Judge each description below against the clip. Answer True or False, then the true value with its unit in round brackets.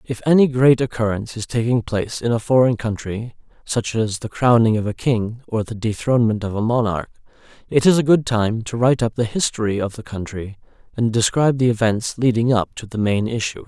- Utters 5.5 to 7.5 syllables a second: True (5.6 syllables/s)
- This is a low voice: True (115 Hz)